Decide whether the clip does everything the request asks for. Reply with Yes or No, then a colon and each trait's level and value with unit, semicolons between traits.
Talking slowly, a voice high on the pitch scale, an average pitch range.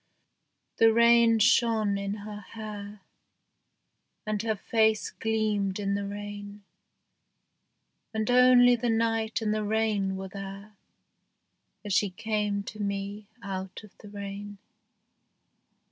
No: slow, 115 wpm; high, 210 Hz; narrow, 1.7 semitones